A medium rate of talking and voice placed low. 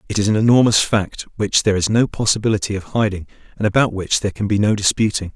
No: fast, 225 wpm; low, 105 Hz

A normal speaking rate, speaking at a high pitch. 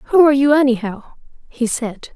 Yes: average, 165 wpm; very high, 255 Hz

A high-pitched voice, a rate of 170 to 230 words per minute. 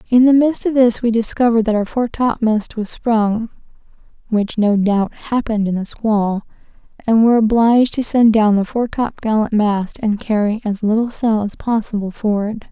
Yes: high, 220 Hz; average, 185 wpm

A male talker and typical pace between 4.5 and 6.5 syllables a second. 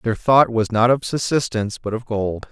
Yes: male; 5.0 syllables/s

